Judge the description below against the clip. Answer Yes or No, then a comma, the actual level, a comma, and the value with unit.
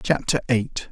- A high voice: No, low, 120 Hz